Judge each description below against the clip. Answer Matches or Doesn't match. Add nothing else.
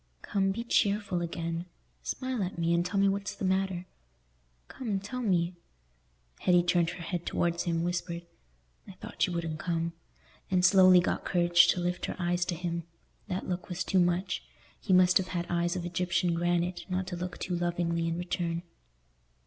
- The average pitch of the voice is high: Doesn't match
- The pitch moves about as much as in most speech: Doesn't match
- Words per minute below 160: Doesn't match